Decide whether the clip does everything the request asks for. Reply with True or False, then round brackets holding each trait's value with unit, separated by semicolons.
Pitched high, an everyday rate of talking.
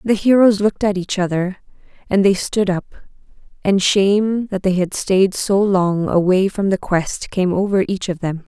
True (195 Hz; 190 wpm)